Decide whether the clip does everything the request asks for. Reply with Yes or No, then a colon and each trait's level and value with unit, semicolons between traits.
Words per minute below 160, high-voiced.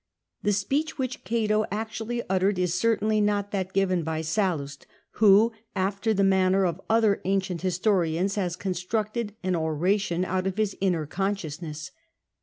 Yes: average, 145 wpm; high, 195 Hz